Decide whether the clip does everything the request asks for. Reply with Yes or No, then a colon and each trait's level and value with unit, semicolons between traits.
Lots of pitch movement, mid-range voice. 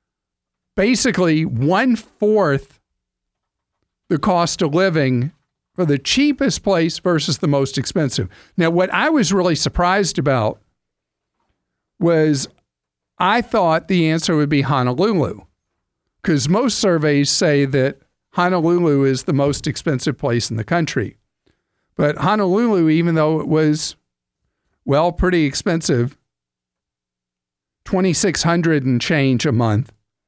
Yes: wide, 6.2 semitones; medium, 150 Hz